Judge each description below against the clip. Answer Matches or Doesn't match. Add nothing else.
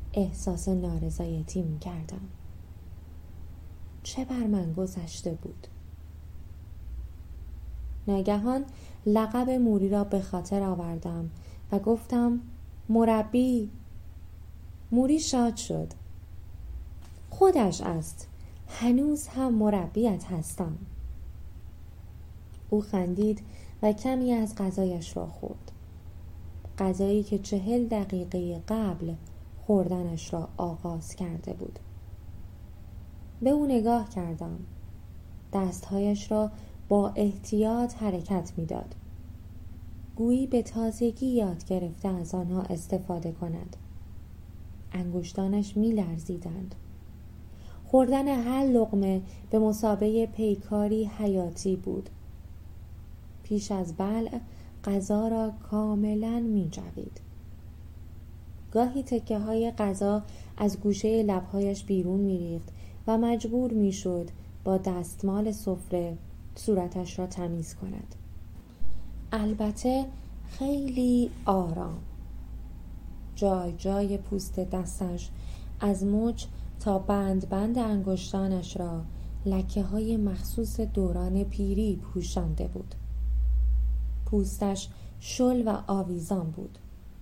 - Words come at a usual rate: Doesn't match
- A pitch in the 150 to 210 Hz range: Matches